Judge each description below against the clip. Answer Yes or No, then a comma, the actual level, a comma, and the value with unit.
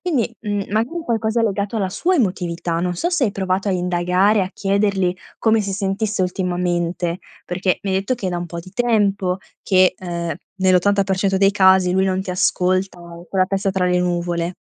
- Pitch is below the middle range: No, high, 190 Hz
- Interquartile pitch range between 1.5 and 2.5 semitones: Yes, narrow, 2.2 semitones